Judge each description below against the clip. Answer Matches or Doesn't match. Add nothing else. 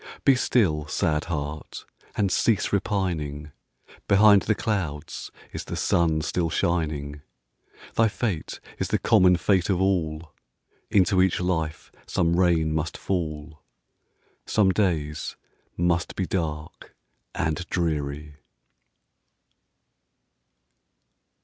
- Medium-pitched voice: Doesn't match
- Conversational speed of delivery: Doesn't match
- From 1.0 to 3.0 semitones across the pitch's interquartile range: Doesn't match